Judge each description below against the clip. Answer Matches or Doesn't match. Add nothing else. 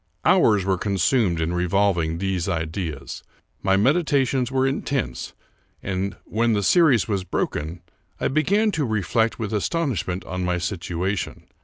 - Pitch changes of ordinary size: Doesn't match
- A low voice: Matches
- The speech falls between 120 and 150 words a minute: Matches